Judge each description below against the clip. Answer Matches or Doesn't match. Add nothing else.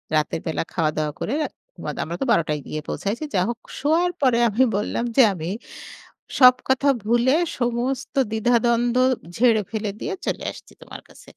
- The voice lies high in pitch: Matches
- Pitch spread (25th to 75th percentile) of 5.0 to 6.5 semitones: Matches